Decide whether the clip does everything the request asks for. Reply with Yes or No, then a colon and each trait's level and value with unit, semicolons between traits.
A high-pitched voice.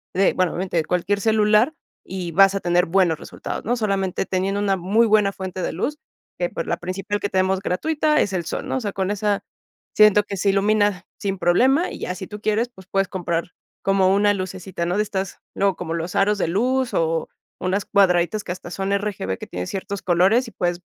Yes: high, 195 Hz